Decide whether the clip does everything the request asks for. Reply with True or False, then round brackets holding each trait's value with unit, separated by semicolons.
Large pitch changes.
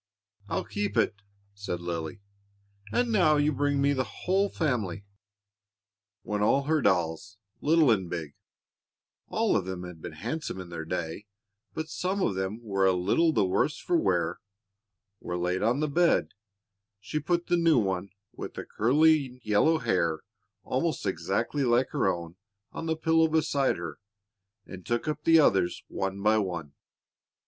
True (8.9 semitones)